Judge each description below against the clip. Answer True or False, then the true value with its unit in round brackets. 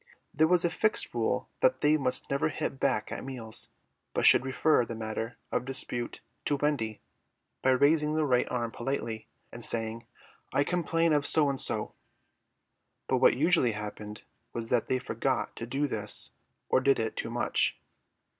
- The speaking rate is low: False (170 wpm)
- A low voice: True (130 Hz)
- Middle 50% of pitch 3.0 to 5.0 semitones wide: True (4.5 semitones)